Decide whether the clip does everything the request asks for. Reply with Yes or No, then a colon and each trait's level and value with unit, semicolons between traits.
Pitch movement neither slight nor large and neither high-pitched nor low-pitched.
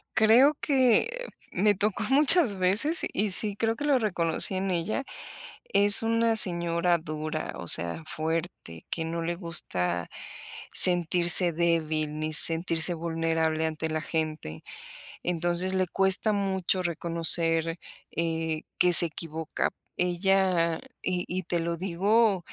Yes: average, 3.3 semitones; medium, 175 Hz